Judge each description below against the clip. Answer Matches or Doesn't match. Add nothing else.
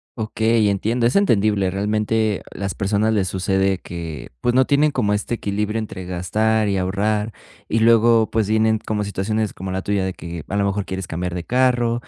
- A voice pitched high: Doesn't match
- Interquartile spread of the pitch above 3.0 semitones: Doesn't match